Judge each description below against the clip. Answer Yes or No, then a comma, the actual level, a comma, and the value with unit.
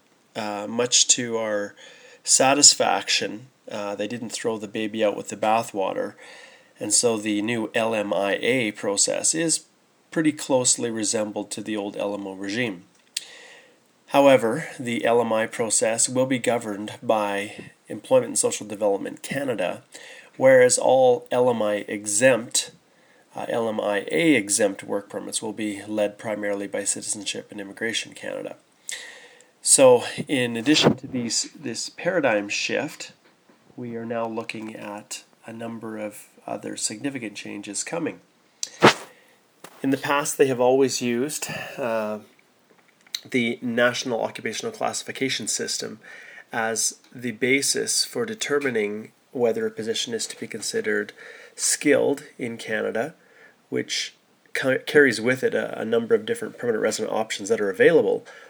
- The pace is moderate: No, slow, 125 wpm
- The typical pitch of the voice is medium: No, low, 125 Hz